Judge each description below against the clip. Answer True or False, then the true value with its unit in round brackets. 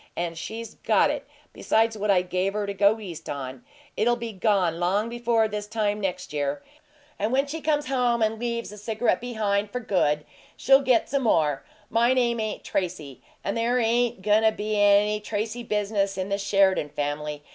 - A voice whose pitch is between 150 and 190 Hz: False (210 Hz)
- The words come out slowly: False (190 wpm)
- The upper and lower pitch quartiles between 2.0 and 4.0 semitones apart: True (3.6 semitones)